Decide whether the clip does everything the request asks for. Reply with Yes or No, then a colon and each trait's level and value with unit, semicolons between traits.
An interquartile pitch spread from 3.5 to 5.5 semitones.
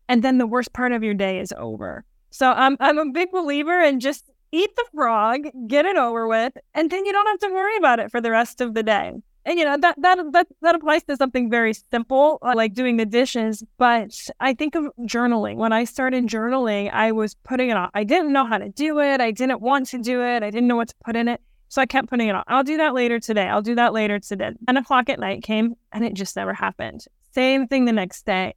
Yes: average, 4.0 semitones